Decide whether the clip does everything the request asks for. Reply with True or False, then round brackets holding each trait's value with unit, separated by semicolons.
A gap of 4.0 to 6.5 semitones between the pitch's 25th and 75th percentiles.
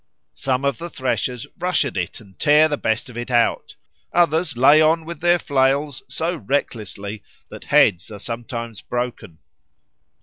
True (5.1 semitones)